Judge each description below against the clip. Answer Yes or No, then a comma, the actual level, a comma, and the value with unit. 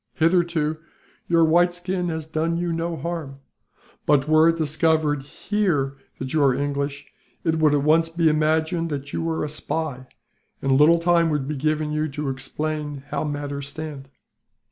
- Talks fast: No, average, 165 wpm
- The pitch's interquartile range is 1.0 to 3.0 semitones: Yes, narrow, 2.4 semitones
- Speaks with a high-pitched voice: No, medium, 155 Hz